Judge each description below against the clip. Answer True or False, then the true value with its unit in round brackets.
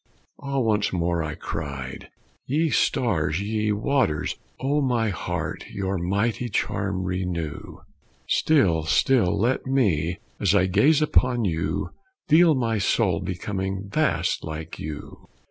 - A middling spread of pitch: False (6.2 semitones)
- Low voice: True (100 Hz)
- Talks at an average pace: False (125 wpm)